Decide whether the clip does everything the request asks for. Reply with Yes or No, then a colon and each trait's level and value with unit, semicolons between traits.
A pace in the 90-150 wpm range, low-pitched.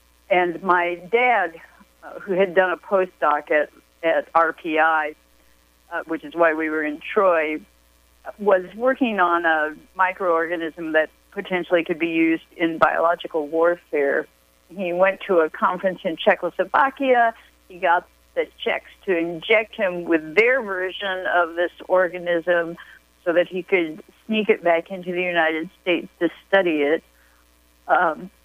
No: average, 140 wpm; medium, 175 Hz